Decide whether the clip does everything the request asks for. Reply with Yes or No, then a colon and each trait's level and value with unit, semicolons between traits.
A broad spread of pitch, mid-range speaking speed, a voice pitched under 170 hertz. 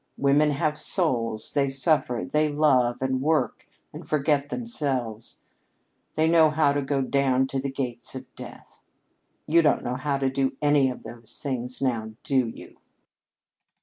No: average, 2.8 semitones; average, 155 wpm; low, 135 Hz